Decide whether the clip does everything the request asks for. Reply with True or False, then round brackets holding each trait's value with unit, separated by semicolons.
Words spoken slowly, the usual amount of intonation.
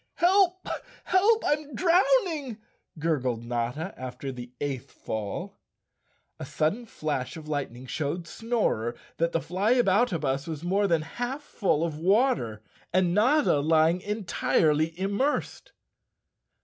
False (115 wpm; 8.9 semitones)